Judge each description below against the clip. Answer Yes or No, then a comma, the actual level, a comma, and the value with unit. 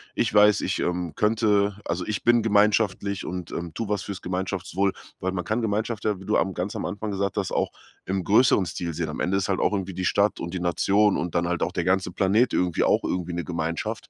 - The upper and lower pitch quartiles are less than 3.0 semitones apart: Yes, narrow, 2.6 semitones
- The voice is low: Yes, very low, 95 Hz